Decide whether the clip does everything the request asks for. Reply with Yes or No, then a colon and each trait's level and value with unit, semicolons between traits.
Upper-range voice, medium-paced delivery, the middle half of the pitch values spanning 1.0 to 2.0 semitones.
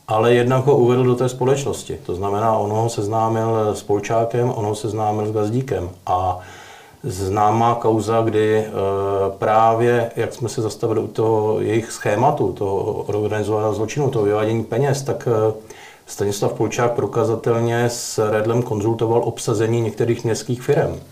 No: low, 115 Hz; average, 140 wpm; narrow, 1.7 semitones